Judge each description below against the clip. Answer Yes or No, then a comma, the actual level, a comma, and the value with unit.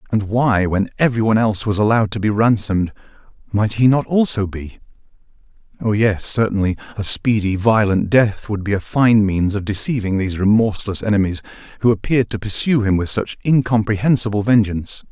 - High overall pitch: No, low, 105 Hz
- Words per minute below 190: Yes, average, 165 wpm